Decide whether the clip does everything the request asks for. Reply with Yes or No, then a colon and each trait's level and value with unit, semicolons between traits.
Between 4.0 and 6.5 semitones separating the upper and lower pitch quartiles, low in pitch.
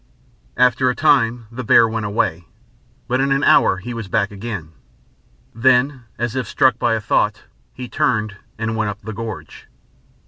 No: average, 3.0 semitones; low, 115 Hz